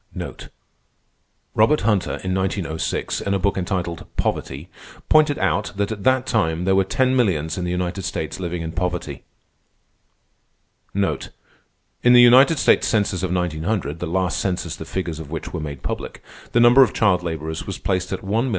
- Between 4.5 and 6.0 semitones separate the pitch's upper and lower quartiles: No, average, 4.1 semitones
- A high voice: No, very low, 95 Hz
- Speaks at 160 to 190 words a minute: Yes, average, 170 wpm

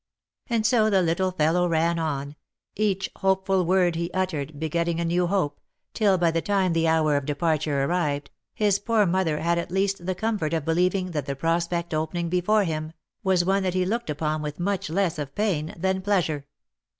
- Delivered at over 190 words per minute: Yes, average, 200 wpm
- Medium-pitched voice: Yes, medium, 170 Hz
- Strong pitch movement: No, average, 3.3 semitones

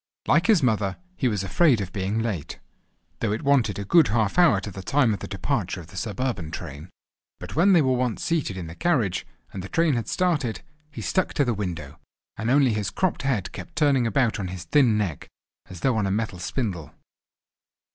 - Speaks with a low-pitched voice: Yes, low, 110 Hz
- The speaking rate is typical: No, fast, 210 wpm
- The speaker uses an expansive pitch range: Yes, wide, 6.5 semitones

